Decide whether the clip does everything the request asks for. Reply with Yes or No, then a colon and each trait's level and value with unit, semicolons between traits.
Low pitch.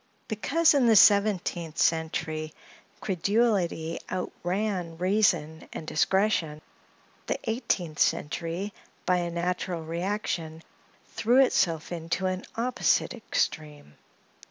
No: medium, 180 Hz